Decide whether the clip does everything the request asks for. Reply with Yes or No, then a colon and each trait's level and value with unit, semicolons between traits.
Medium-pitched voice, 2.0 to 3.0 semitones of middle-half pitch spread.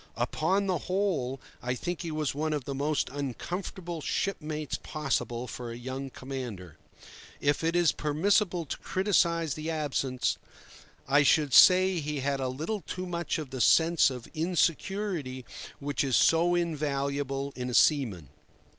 No: medium, 150 Hz; average, 4.3 semitones